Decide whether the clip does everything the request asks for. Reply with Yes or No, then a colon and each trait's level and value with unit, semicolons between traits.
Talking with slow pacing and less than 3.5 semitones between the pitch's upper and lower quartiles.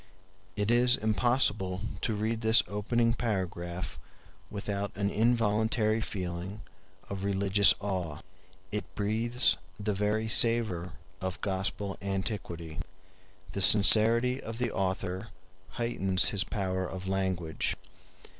Yes: slow, 110 wpm; average, 3.0 semitones